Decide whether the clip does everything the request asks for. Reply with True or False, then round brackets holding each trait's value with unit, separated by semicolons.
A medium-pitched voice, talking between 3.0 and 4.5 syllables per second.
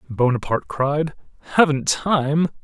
True (145 Hz; 4.2 syllables/s)